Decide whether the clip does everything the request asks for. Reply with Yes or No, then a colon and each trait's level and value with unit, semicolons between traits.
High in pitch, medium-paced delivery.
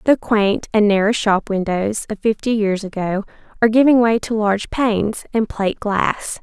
Yes: high, 215 Hz; average, 175 wpm